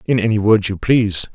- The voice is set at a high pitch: No, low, 105 Hz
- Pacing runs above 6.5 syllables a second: No, 5.7 syllables/s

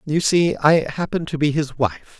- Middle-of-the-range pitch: Yes, medium, 150 Hz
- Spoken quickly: Yes, fast, 220 wpm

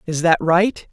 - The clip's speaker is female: No, male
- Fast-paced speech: No, average, 195 wpm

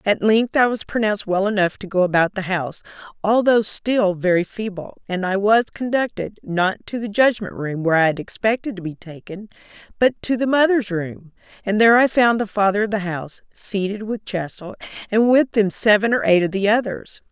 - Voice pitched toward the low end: No, high, 205 Hz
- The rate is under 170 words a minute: No, average, 200 wpm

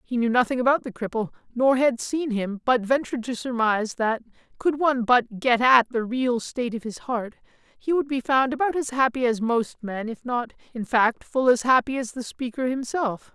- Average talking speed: No, fast, 210 wpm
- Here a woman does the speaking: No, male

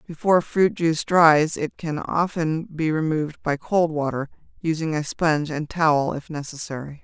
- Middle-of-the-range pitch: Yes, medium, 155 Hz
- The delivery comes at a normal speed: Yes, average, 160 wpm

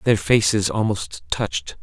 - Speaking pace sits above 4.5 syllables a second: No, 4.0 syllables/s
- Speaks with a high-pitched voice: No, low, 100 Hz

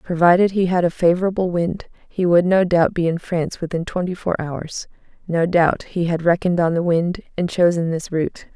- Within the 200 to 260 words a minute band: Yes, fast, 205 wpm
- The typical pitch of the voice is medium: Yes, medium, 175 Hz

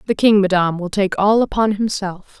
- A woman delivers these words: Yes, female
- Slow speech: No, average, 200 wpm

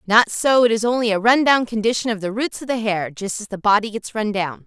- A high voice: Yes, high, 220 Hz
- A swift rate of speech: Yes, fast, 270 wpm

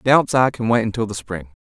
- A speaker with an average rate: No, fast, 255 wpm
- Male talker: Yes, male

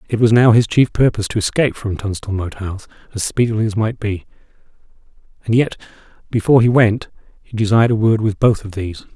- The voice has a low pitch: Yes, low, 110 Hz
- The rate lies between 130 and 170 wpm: No, average, 195 wpm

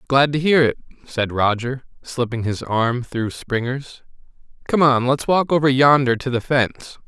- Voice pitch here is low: Yes, low, 130 Hz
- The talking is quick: No, average, 170 wpm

